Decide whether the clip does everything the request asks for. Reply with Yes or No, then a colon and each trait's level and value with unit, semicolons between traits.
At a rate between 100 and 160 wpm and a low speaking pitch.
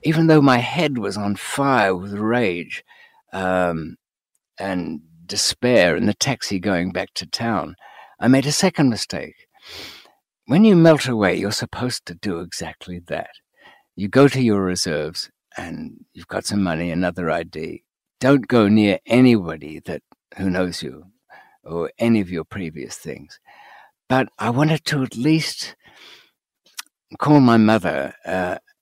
Yes: average, 145 wpm; low, 110 Hz